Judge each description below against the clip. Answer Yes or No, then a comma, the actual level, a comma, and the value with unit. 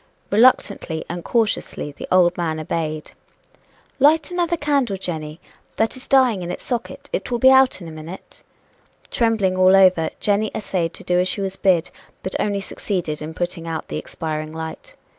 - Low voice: No, medium, 185 Hz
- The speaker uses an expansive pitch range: Yes, wide, 5.7 semitones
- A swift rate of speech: No, average, 175 wpm